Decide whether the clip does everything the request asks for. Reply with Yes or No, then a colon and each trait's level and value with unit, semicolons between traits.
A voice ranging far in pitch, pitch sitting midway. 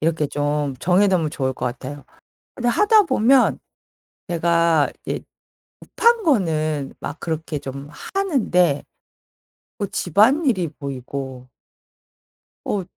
Yes: wide, 6.8 semitones; medium, 165 Hz